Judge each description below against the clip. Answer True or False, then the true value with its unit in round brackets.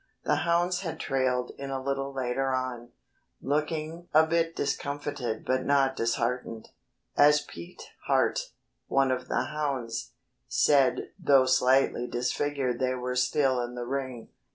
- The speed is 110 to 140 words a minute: True (135 wpm)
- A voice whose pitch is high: False (135 Hz)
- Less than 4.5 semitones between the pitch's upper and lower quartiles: True (2.4 semitones)